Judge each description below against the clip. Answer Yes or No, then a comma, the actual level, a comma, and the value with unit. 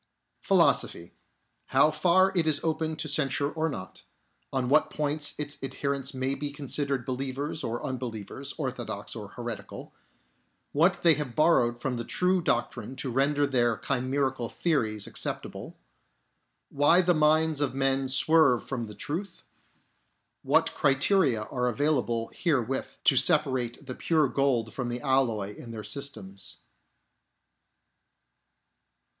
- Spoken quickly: No, average, 140 wpm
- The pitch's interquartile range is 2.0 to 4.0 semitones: Yes, average, 3.6 semitones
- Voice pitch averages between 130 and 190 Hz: Yes, low, 135 Hz